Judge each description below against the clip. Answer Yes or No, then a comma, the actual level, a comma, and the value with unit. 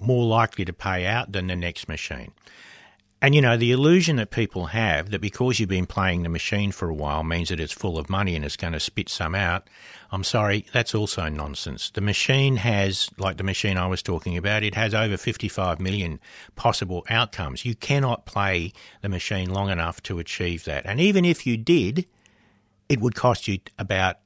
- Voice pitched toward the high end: No, low, 100 Hz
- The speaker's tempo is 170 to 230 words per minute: Yes, fast, 205 wpm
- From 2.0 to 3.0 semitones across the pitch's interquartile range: No, average, 4.1 semitones